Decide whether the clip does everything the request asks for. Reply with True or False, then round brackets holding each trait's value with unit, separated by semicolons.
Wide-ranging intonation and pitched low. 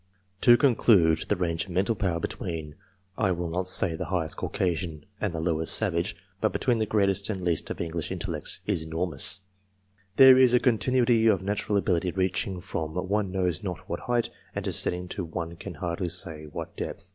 False (3.7 semitones; 90 Hz)